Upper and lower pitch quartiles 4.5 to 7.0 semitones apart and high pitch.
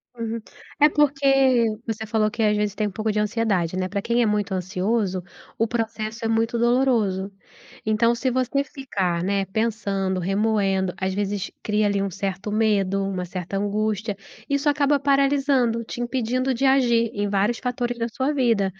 No: average, 3.4 semitones; high, 220 Hz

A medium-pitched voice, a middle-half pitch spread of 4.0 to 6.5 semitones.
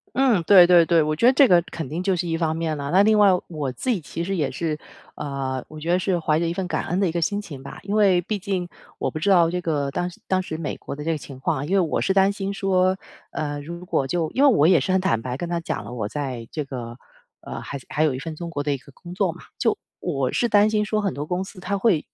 Yes: medium, 170 Hz; average, 4.4 semitones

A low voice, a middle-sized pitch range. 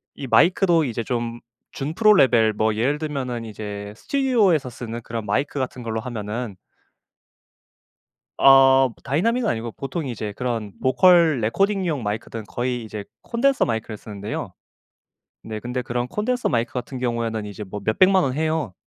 No: low, 125 Hz; wide, 5.7 semitones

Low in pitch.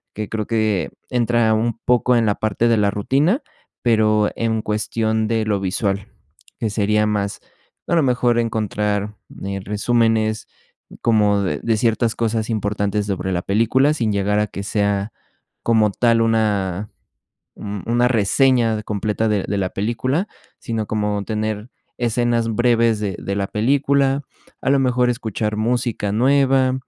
Yes: low, 110 Hz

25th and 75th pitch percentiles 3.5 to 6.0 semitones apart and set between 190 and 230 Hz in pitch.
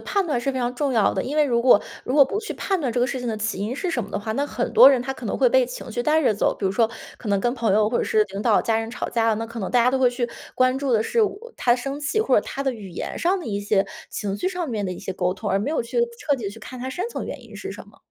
No: average, 4.3 semitones; high, 245 Hz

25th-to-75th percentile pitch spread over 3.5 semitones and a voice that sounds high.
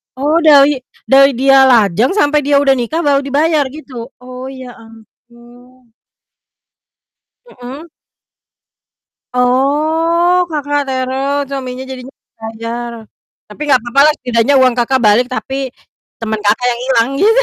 No: average, 3.1 semitones; very high, 260 Hz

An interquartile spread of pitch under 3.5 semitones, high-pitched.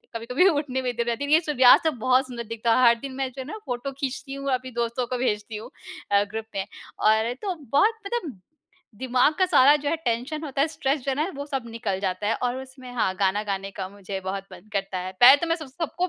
No: average, 4.4 semitones; very high, 255 Hz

